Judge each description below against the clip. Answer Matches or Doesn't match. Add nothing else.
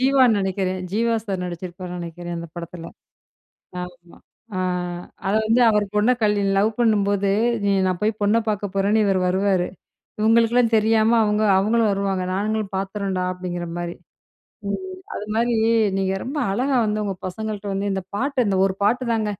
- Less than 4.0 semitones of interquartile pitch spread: Matches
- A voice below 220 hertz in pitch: Matches